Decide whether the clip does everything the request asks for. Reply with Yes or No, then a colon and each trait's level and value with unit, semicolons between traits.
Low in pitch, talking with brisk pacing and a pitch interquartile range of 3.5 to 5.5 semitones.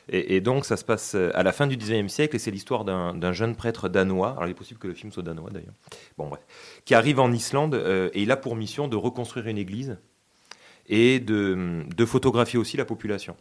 Yes: low, 110 Hz; fast, 235 wpm; average, 4.6 semitones